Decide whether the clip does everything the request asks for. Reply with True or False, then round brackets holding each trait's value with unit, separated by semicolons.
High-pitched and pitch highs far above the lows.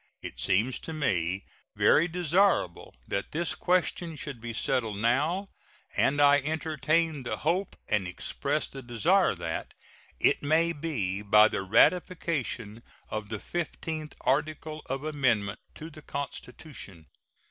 False (145 Hz; 6.5 semitones)